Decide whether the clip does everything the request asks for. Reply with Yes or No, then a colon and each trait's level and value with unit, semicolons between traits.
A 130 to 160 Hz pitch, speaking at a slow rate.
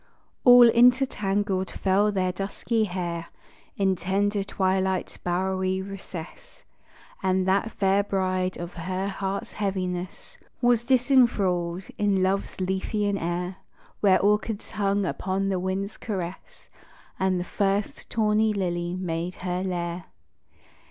No: high, 190 Hz; slow, 115 wpm